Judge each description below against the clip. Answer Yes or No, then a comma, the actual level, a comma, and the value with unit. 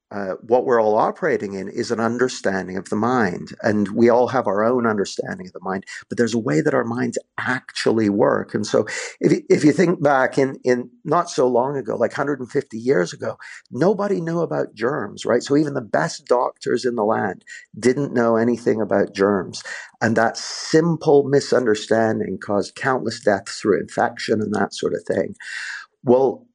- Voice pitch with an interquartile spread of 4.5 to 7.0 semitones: Yes, average, 5.1 semitones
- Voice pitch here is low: Yes, low, 125 Hz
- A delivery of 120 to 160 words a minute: No, average, 190 wpm